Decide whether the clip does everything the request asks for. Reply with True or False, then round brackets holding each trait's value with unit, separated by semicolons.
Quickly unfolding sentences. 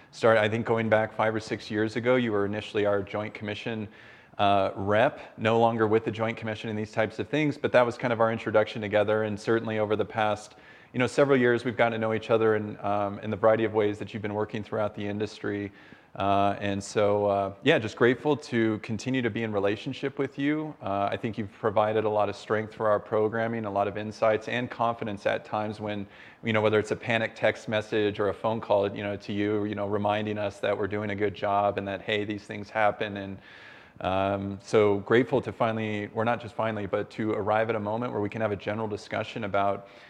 True (235 wpm)